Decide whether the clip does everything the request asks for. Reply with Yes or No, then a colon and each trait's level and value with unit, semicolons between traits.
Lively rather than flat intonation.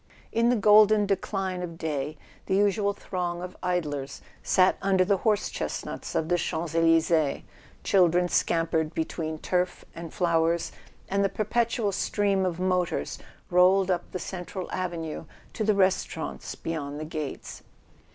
No: average, 3.1 semitones